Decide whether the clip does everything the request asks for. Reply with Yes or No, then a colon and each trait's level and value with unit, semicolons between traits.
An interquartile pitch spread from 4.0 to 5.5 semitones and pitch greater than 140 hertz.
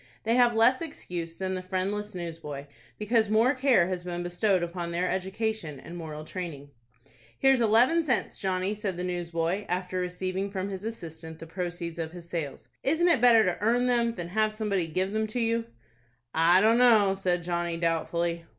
Yes: average, 4.3 semitones; medium, 185 Hz